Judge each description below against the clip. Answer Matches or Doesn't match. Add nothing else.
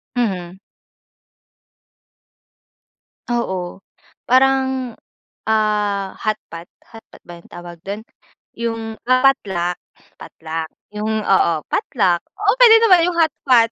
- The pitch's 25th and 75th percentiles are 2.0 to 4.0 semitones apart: Doesn't match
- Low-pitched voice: Doesn't match